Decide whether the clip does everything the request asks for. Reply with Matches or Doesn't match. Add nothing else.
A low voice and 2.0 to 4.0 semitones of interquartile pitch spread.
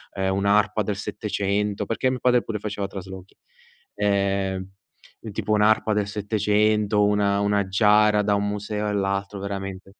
Doesn't match